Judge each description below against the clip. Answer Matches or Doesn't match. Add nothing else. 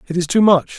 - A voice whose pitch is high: Doesn't match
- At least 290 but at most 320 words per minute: Matches